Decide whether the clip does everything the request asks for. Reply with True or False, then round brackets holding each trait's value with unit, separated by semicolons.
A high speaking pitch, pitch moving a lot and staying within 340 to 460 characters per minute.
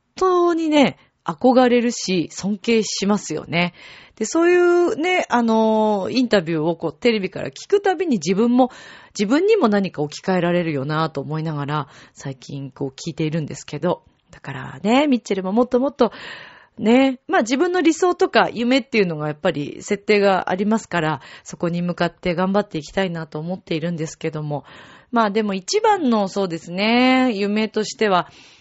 True (205 Hz; 7.0 semitones; 365 characters per minute)